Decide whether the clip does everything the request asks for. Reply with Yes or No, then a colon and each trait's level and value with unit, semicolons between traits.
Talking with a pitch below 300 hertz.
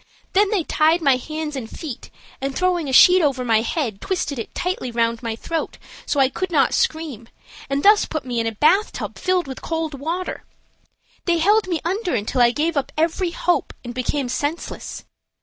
No: very high, 305 Hz